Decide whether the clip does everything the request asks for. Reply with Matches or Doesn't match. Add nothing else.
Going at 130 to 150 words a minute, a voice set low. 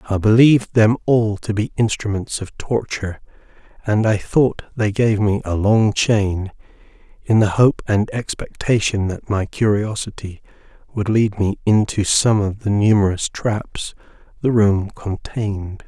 Matches